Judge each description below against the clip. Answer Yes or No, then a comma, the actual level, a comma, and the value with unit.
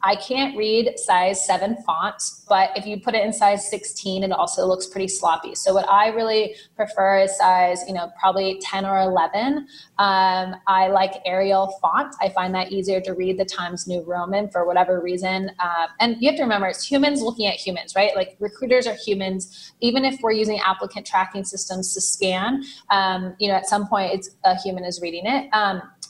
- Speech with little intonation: Yes, narrow, 2.1 semitones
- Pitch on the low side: No, high, 195 Hz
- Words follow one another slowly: No, average, 200 wpm